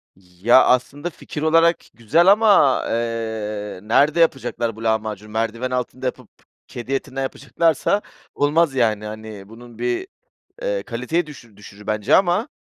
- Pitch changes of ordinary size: No, wide, 5.7 semitones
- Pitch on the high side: No, low, 120 Hz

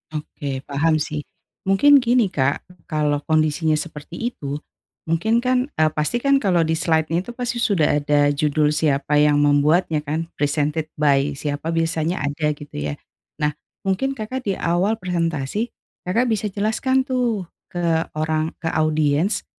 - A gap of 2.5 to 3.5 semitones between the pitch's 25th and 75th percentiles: No, average, 4.7 semitones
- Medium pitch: Yes, medium, 160 Hz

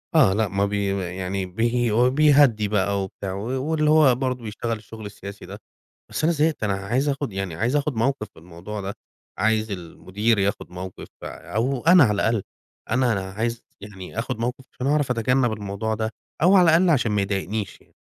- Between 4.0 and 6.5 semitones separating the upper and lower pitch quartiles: Yes, average, 4.5 semitones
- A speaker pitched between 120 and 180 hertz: No, low, 110 Hz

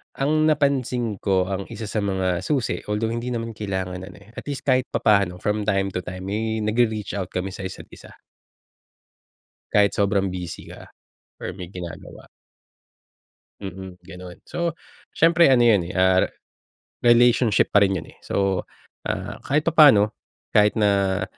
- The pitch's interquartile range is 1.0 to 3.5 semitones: No, average, 3.9 semitones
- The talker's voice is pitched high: No, low, 105 Hz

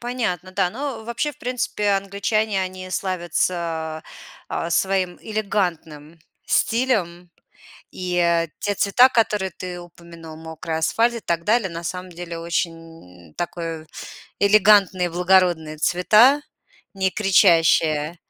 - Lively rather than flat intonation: No, average, 3.7 semitones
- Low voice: No, medium, 180 Hz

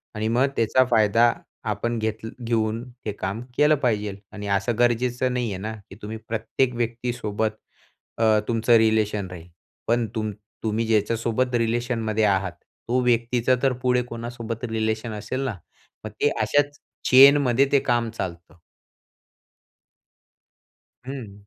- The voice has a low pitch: Yes, low, 115 Hz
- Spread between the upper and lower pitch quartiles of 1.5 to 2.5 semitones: Yes, narrow, 2.1 semitones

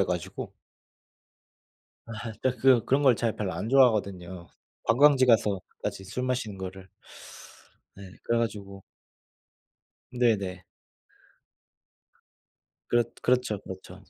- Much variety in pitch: No, average, 4.4 semitones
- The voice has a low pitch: Yes, low, 110 Hz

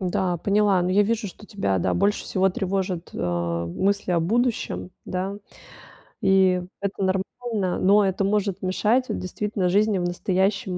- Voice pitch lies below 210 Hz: Yes, high, 190 Hz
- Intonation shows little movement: Yes, narrow, 2.1 semitones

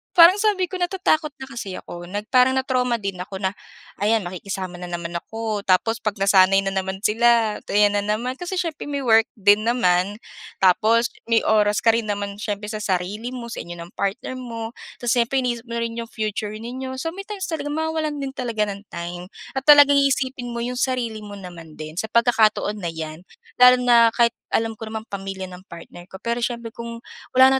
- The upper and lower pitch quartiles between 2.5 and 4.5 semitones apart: Yes, average, 4.2 semitones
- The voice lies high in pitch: Yes, high, 225 Hz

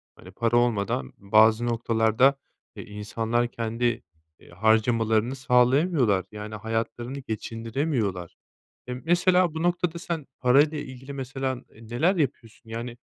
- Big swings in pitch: No, average, 3.5 semitones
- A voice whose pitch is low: Yes, low, 120 Hz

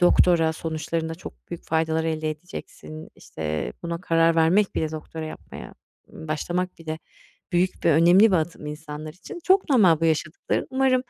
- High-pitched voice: No, medium, 165 Hz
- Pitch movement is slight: Yes, narrow, 2.2 semitones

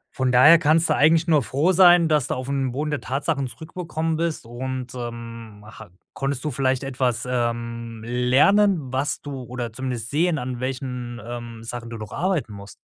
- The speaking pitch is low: Yes, low, 130 Hz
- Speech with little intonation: No, average, 4.1 semitones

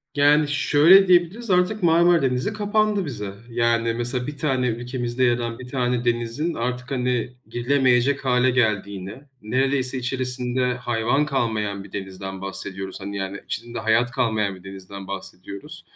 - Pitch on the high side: No, low, 125 Hz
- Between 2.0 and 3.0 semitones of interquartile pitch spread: No, average, 4.1 semitones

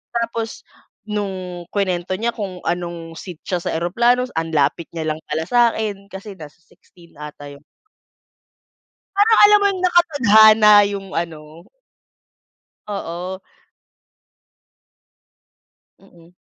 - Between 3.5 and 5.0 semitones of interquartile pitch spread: Yes, average, 4.6 semitones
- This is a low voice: No, high, 190 Hz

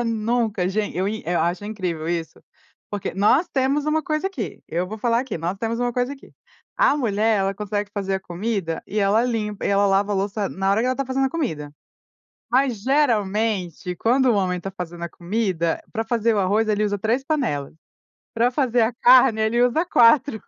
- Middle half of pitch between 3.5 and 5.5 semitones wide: Yes, average, 4.1 semitones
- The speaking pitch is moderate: No, high, 215 Hz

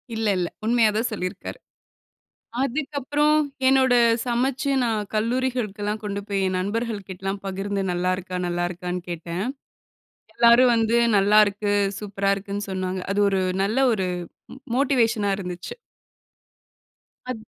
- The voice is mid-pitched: No, high, 205 Hz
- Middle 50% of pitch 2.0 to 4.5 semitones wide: Yes, average, 3.7 semitones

